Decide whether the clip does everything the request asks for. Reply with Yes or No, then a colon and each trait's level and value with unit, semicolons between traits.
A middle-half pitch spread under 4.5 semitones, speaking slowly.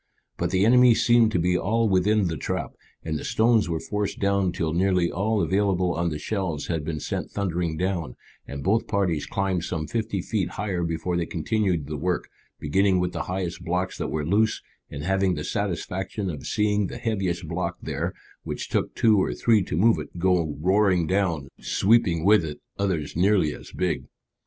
No: average, 3.4 semitones; average, 190 wpm